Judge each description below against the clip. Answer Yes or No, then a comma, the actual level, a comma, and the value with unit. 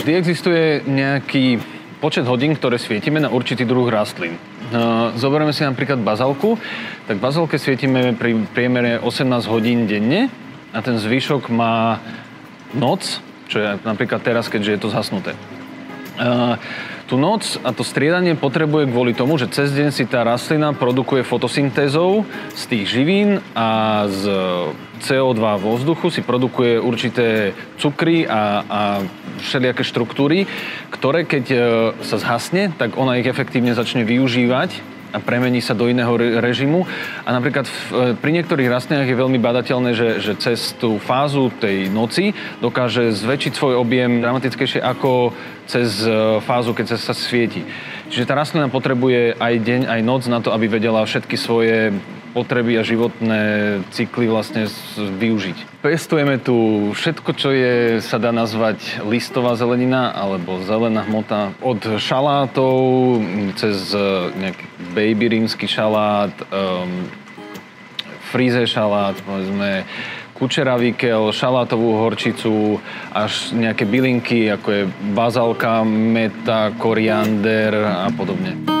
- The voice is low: Yes, low, 120 Hz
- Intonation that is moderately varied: Yes, average, 3.1 semitones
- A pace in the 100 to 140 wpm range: Yes, average, 130 wpm